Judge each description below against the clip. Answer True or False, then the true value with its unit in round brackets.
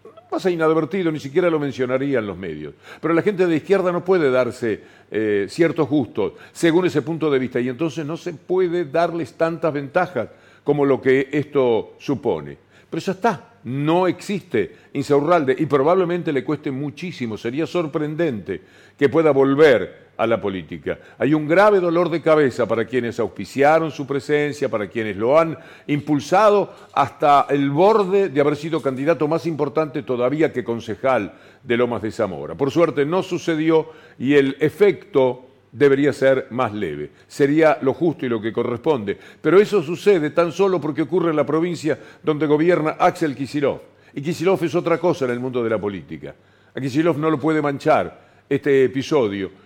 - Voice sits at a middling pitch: True (150 Hz)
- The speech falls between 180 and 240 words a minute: False (170 wpm)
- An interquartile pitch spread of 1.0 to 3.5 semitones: False (4.3 semitones)